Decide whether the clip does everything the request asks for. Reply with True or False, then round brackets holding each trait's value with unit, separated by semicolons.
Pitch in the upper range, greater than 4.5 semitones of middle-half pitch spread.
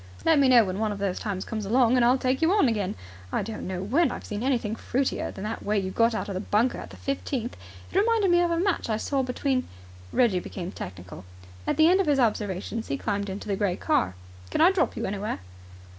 True (225 Hz; 5.4 semitones)